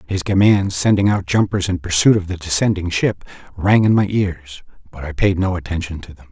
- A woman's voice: No, male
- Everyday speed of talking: No, fast, 210 wpm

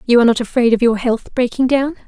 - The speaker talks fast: Yes, fast, 260 wpm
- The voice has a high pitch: Yes, high, 245 Hz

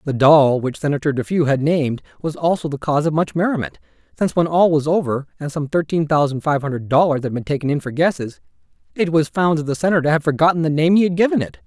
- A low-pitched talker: No, medium, 150 Hz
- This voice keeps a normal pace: No, fast, 235 wpm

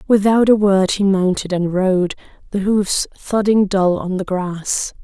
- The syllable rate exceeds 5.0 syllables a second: No, 3.9 syllables/s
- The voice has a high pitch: Yes, high, 195 Hz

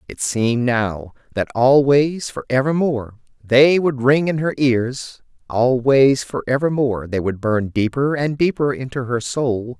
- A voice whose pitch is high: No, low, 130 Hz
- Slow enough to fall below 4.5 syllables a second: Yes, 4.2 syllables/s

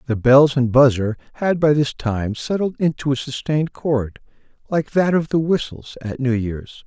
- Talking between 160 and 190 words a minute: Yes, average, 185 wpm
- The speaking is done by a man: Yes, male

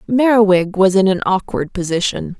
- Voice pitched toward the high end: Yes, high, 195 Hz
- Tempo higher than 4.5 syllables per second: Yes, 5.0 syllables/s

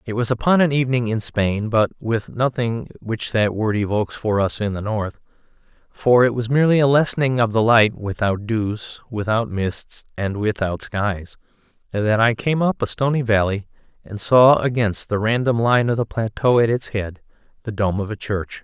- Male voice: Yes, male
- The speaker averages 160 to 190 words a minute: Yes, average, 185 wpm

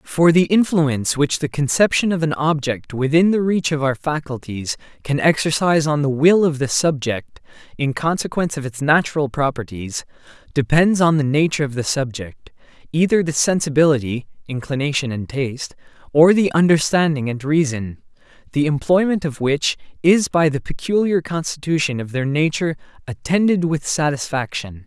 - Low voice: No, medium, 150 Hz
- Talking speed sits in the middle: Yes, average, 150 wpm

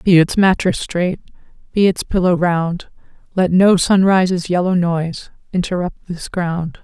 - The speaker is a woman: Yes, female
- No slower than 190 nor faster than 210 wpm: No, average, 140 wpm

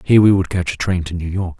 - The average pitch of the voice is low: Yes, very low, 90 Hz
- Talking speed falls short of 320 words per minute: No, fast, 340 wpm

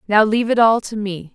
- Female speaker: Yes, female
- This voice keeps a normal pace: No, fast, 270 wpm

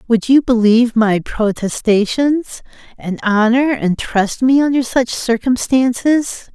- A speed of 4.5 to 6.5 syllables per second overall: No, 3.9 syllables/s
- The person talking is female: Yes, female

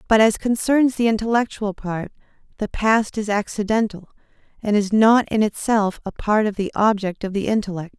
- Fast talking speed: No, average, 175 wpm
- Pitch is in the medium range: No, high, 210 Hz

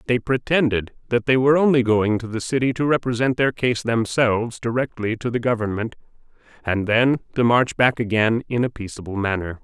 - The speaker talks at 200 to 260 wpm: No, average, 180 wpm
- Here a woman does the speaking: No, male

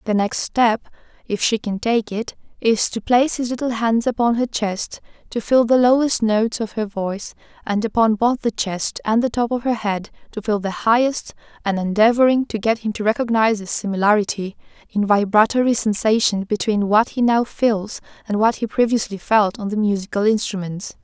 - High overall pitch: Yes, high, 220 Hz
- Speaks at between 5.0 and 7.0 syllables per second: Yes, 5.2 syllables/s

